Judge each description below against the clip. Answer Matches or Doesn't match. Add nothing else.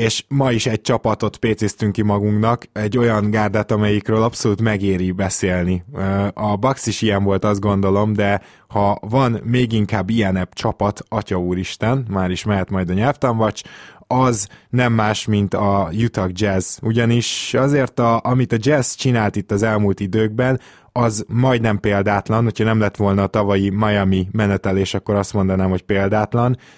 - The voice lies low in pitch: Matches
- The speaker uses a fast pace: Matches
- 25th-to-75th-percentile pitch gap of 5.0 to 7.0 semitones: Doesn't match